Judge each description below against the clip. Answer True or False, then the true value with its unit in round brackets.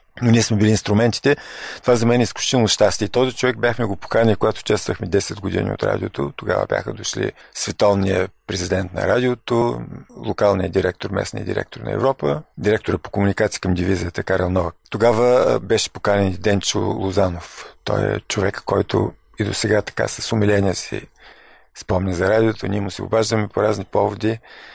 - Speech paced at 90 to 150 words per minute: False (165 wpm)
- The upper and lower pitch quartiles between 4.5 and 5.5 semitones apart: False (3.3 semitones)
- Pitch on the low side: True (105 Hz)